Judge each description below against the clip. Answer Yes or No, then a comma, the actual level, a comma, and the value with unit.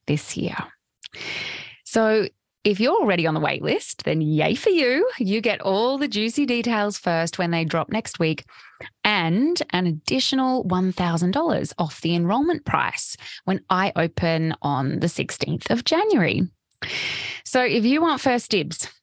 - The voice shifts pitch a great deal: Yes, wide, 6.7 semitones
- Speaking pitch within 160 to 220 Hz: Yes, high, 190 Hz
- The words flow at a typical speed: Yes, average, 150 wpm